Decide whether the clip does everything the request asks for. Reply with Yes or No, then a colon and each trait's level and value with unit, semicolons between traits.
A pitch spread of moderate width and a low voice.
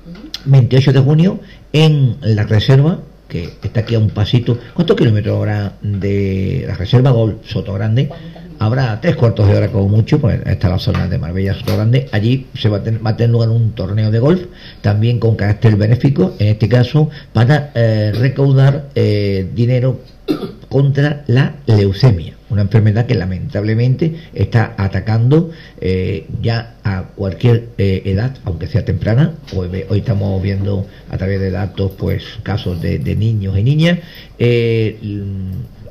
Yes: average, 4.5 semitones; low, 115 Hz